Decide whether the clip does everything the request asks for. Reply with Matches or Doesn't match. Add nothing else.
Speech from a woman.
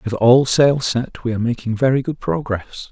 Doesn't match